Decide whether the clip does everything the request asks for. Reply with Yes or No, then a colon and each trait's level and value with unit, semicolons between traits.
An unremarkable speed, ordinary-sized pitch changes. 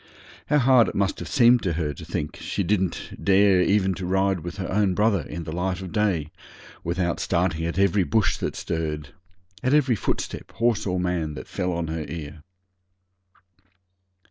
Yes: average, 180 wpm; average, 3.5 semitones